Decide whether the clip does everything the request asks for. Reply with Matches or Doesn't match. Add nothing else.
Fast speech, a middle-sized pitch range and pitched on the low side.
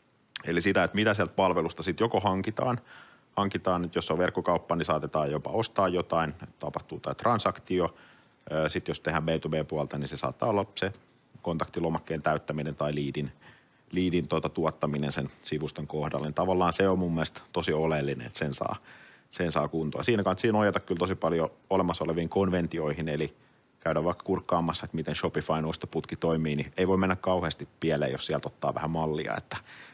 Matches